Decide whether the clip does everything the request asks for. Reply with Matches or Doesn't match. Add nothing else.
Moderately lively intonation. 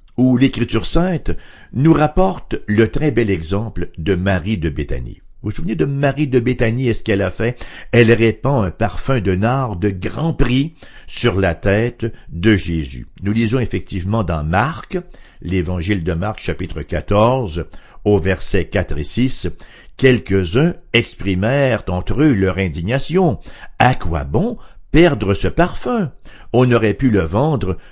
Doesn't match